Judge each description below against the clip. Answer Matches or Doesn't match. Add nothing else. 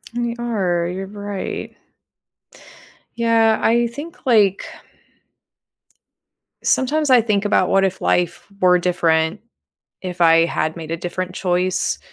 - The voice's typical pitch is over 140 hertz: Matches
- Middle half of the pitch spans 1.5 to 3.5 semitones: Doesn't match